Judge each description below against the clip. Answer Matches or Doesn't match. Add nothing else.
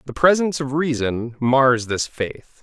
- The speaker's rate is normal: Matches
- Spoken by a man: Matches